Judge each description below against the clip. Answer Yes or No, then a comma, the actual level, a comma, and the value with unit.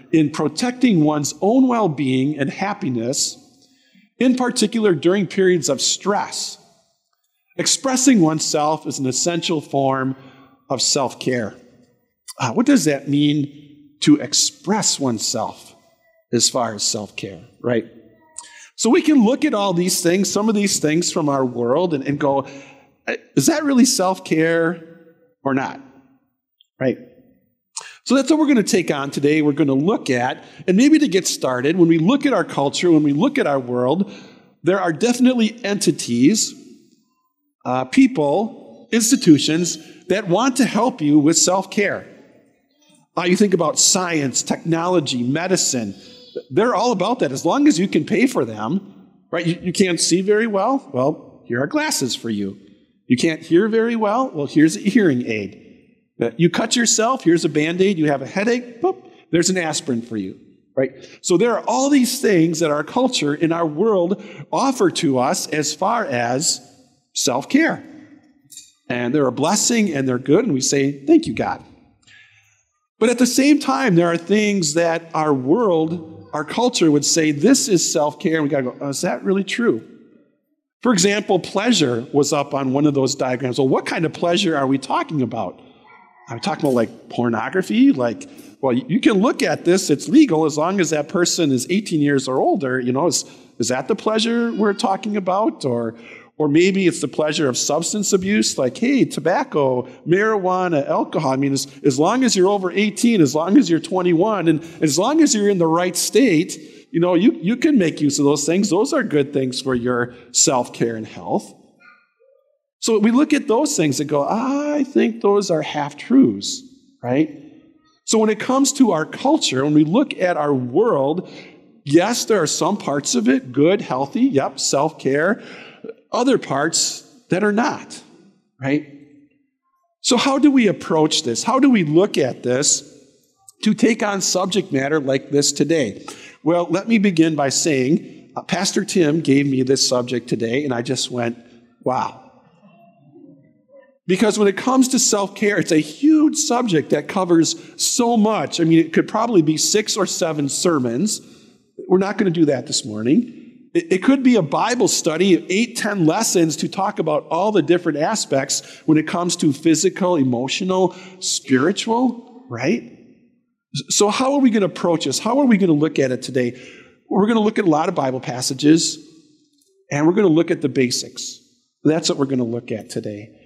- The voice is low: No, medium, 175 Hz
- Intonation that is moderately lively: No, wide, 8.3 semitones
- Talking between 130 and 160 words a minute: No, average, 180 wpm